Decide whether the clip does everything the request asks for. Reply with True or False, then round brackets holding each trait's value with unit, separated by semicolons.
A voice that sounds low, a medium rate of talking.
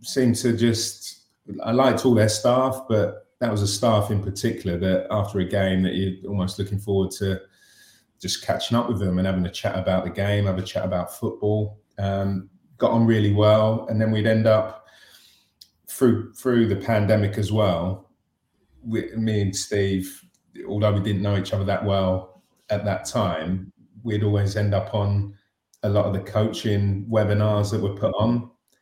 True (105 Hz; 185 wpm)